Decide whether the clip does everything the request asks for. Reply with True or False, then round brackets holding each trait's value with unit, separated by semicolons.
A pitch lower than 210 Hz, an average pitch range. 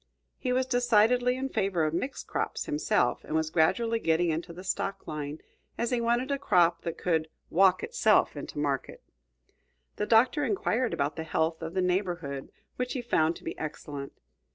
False (185 Hz; 7.3 semitones)